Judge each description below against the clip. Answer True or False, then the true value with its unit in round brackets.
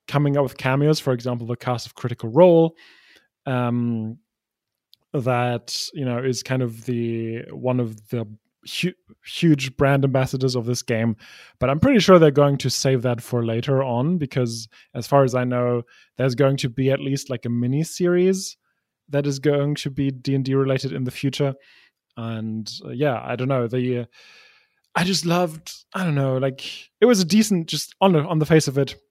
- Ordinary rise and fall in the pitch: True (3.5 semitones)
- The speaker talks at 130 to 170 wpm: False (195 wpm)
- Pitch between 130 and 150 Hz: True (135 Hz)